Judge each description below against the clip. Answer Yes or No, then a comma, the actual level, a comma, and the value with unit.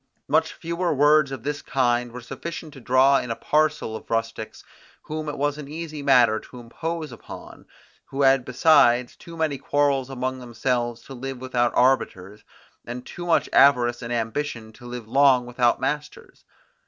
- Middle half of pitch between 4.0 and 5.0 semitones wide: No, average, 3.3 semitones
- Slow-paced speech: No, average, 165 wpm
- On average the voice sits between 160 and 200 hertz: No, low, 130 Hz